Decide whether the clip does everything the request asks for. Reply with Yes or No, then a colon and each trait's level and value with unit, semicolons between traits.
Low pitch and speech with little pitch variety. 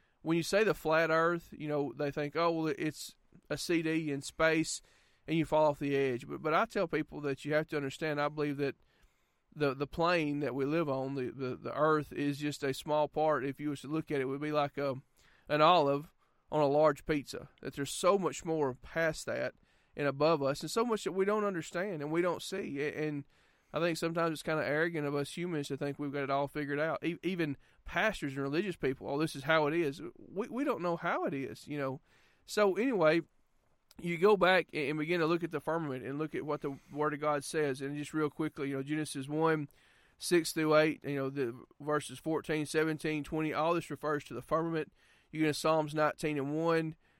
No: medium, 150 Hz; narrow, 2.2 semitones